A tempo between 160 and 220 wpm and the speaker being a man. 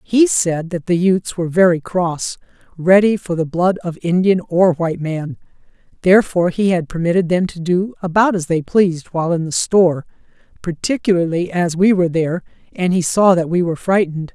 No: average, 175 wpm; female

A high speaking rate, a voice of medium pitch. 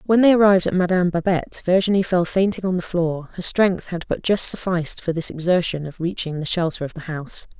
Yes: fast, 220 wpm; medium, 180 Hz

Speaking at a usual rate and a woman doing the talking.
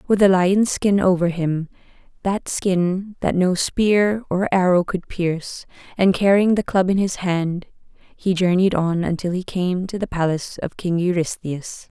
Yes: average, 160 wpm; female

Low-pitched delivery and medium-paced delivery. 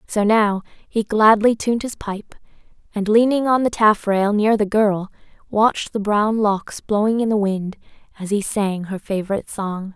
No: high, 210 Hz; average, 175 wpm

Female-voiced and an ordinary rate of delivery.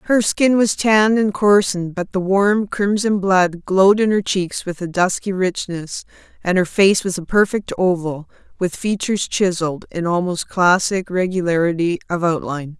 Yes: female; average, 165 wpm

